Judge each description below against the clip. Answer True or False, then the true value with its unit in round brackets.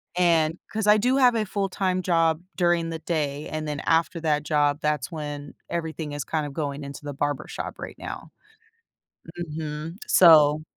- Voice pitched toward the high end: False (160 Hz)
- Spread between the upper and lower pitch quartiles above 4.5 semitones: False (2.7 semitones)